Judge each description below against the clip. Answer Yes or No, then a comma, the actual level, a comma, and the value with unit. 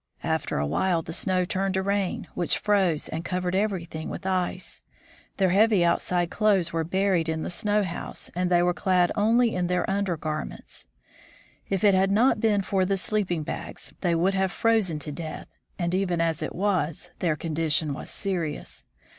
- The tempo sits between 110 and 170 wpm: No, average, 180 wpm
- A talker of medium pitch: Yes, medium, 180 Hz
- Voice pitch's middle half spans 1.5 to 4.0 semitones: Yes, average, 2.8 semitones